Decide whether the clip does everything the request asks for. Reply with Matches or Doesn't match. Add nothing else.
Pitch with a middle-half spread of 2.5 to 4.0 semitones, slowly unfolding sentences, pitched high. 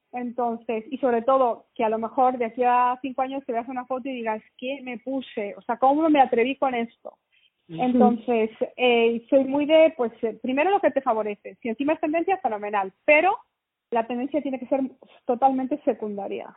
Doesn't match